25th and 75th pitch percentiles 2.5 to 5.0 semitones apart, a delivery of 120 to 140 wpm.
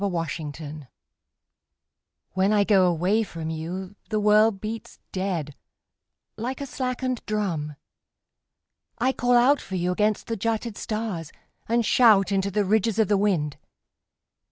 Yes: average, 4.0 semitones; slow, 135 wpm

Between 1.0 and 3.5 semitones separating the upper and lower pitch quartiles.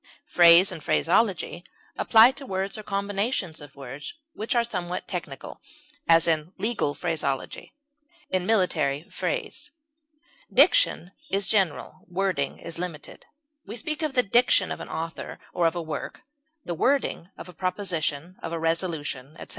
No: average, 4.1 semitones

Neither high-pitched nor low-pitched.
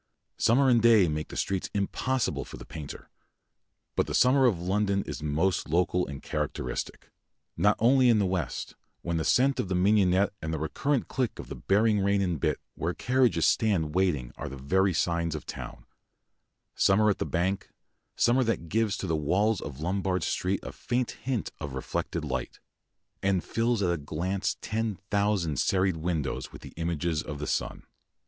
No: very low, 95 Hz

